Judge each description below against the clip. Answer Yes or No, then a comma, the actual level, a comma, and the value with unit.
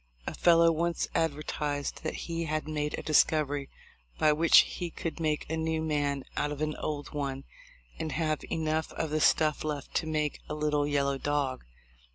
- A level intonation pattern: Yes, narrow, 1.5 semitones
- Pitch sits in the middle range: Yes, medium, 150 Hz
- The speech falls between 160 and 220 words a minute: Yes, average, 180 wpm